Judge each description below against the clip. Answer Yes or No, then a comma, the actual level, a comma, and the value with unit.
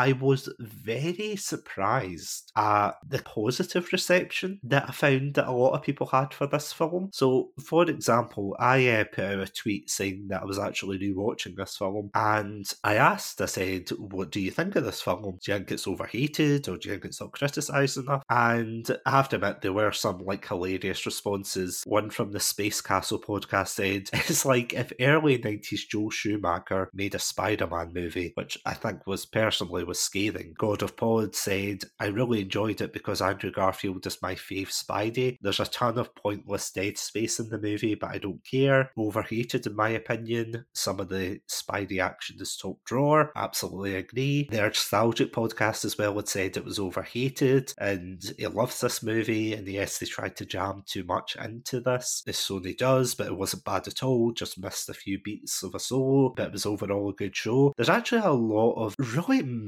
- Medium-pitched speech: No, low, 110 Hz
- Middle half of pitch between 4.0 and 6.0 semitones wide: Yes, average, 4.9 semitones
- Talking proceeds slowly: No, average, 200 wpm